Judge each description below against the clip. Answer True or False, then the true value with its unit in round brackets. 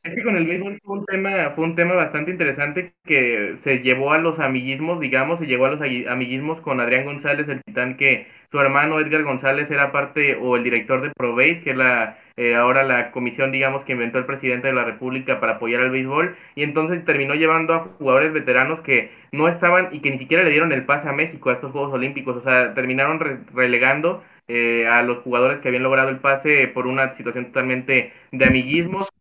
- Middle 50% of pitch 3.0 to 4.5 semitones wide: True (3.8 semitones)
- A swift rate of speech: True (215 wpm)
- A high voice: False (135 Hz)